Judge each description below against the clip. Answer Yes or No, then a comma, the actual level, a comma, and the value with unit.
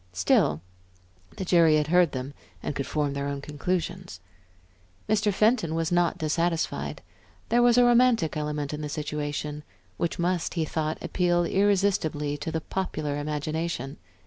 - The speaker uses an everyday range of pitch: Yes, average, 3.4 semitones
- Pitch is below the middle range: No, medium, 160 Hz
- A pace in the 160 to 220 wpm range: No, average, 145 wpm